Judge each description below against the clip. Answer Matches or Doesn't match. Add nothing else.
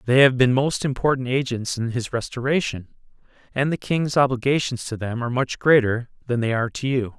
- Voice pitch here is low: Matches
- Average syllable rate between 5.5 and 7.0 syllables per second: Matches